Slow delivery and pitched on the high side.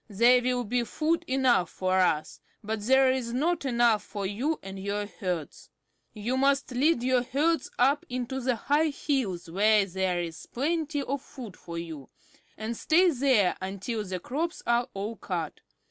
No: average, 165 wpm; high, 240 Hz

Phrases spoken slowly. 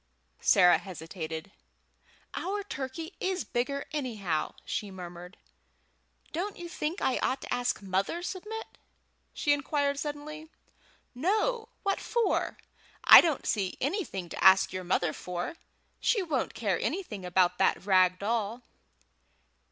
Yes: slow, 125 wpm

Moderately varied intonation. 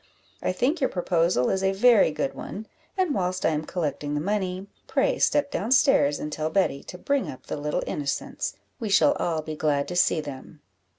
No: wide, 5.7 semitones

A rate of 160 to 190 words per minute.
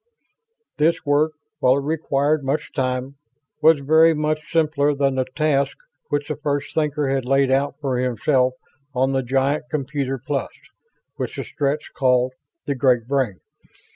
No: average, 150 wpm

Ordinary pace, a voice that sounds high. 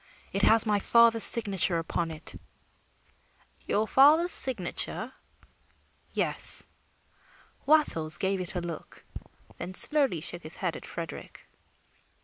No: slow, 115 wpm; high, 195 Hz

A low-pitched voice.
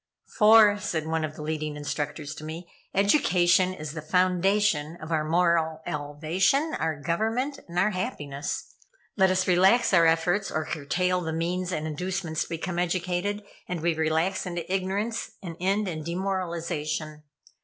No: medium, 175 Hz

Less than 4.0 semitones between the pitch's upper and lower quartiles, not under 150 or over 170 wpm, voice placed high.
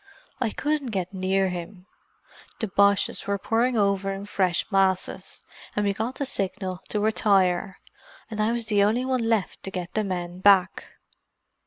Yes: average, 2.7 semitones; average, 155 wpm; high, 200 Hz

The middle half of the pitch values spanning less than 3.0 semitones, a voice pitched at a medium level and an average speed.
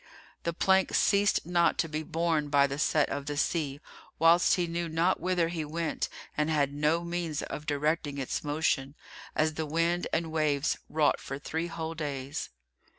Yes: narrow, 2.4 semitones; medium, 160 Hz; average, 175 wpm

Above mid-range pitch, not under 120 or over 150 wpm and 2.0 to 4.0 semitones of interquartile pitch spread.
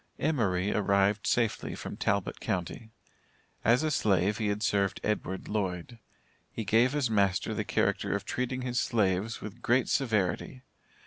No: low, 105 Hz; average, 145 wpm; average, 3.6 semitones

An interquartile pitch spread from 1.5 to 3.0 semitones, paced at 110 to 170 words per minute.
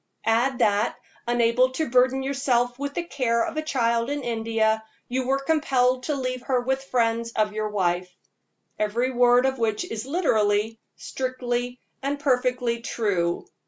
Yes: average, 2.7 semitones; average, 155 wpm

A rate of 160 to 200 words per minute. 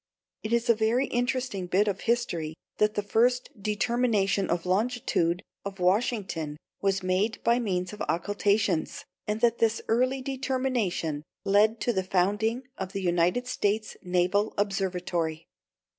No: average, 145 wpm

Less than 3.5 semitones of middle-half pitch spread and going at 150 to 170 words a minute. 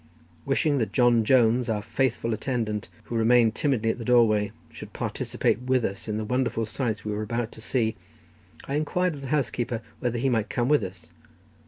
No: average, 2.9 semitones; average, 190 wpm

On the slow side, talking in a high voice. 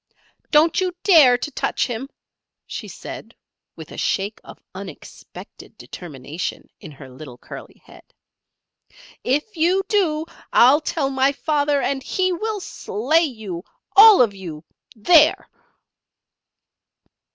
Yes: slow, 120 wpm; very high, 275 Hz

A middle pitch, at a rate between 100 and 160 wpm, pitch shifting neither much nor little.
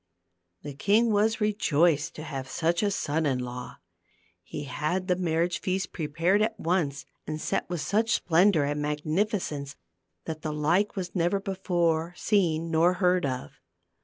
Yes: medium, 170 Hz; average, 155 wpm; average, 4.1 semitones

